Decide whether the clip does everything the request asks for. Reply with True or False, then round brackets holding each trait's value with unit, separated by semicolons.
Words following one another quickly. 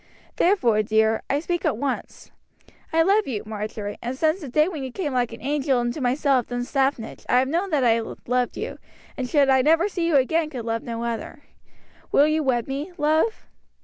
True (210 wpm)